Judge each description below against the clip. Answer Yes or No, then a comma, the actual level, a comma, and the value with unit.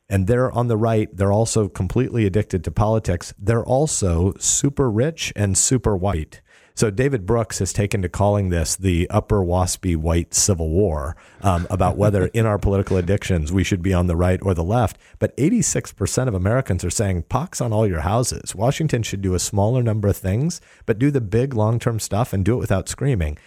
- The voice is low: Yes, low, 100 Hz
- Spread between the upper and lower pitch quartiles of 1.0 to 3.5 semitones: No, average, 3.9 semitones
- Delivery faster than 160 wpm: Yes, average, 200 wpm